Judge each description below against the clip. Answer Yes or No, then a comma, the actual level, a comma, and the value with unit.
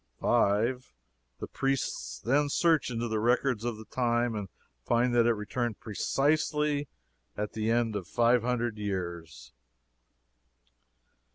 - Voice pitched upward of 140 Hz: No, low, 120 Hz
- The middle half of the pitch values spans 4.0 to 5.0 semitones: No, average, 3.1 semitones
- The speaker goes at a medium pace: No, slow, 125 wpm